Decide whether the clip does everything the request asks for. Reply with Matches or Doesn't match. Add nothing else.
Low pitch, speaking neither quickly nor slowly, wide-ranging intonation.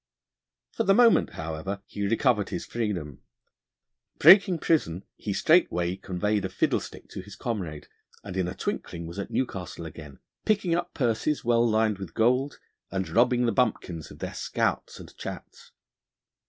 Matches